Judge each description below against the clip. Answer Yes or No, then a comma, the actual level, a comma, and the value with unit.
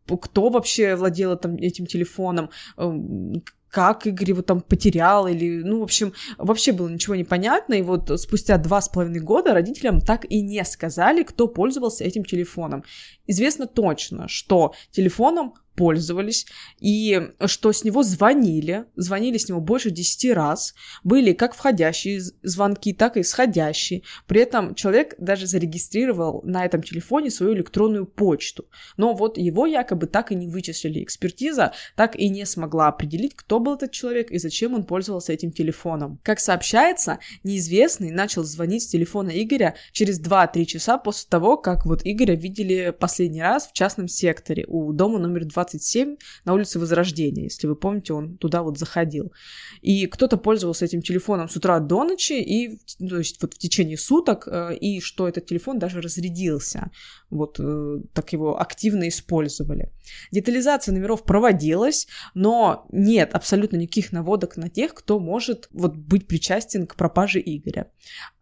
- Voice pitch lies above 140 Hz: Yes, high, 190 Hz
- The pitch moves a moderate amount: Yes, average, 3.9 semitones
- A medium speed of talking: Yes, average, 150 wpm